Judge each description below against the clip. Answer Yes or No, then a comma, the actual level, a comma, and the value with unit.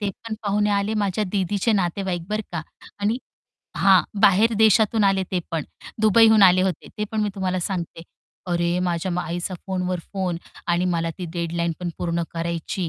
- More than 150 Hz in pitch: Yes, medium, 185 Hz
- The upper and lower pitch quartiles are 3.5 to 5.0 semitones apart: No, average, 3.1 semitones